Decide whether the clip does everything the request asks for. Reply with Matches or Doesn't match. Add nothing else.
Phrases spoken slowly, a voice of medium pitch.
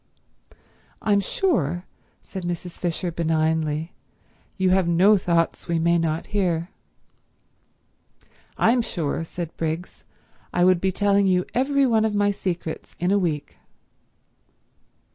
Matches